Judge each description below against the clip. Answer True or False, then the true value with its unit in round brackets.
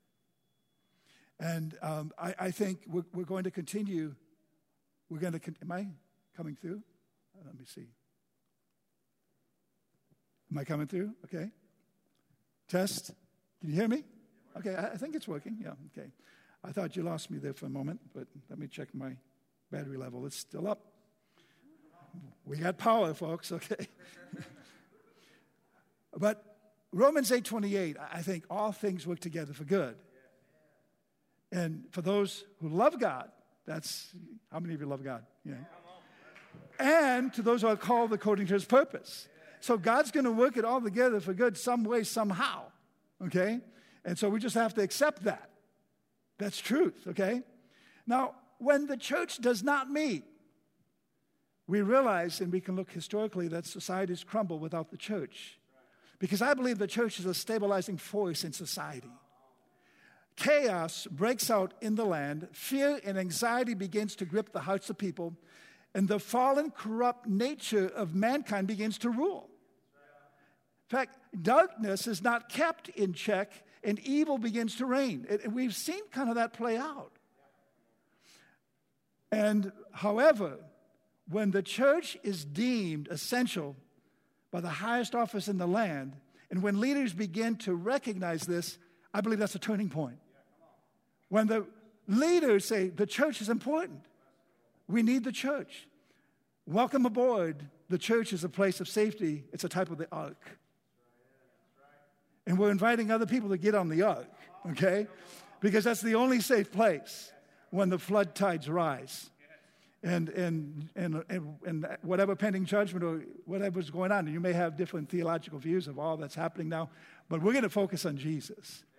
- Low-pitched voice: False (195 Hz)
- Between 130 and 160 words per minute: True (155 wpm)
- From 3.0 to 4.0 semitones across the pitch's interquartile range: False (4.9 semitones)